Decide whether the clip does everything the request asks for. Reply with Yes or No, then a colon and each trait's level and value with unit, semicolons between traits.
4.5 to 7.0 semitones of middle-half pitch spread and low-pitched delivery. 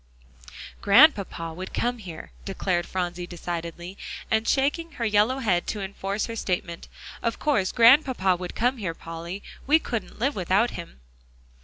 No: average, 5.2 semitones; high, 195 Hz